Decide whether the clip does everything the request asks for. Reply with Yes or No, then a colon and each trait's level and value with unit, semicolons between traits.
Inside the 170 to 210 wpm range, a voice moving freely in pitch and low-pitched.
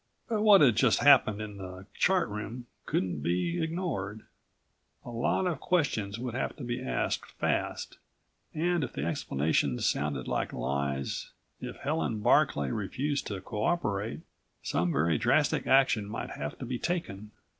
No: average, 150 wpm; wide, 8.2 semitones; low, 110 Hz